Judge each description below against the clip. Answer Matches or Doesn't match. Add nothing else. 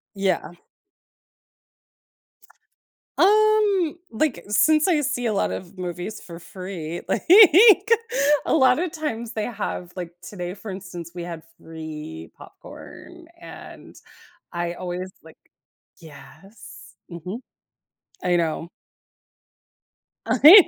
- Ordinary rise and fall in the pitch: Doesn't match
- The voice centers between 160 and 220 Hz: Matches